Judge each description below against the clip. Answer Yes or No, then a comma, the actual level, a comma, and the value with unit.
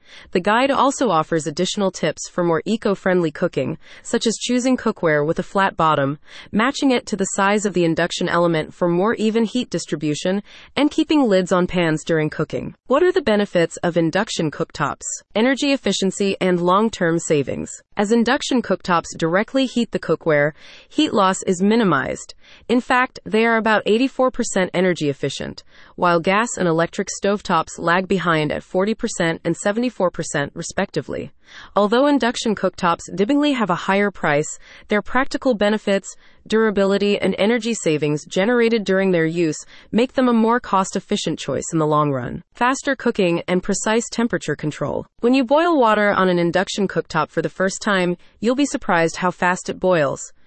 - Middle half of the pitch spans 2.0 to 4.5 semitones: No, average, 5.3 semitones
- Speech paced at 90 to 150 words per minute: No, average, 165 wpm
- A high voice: Yes, high, 195 Hz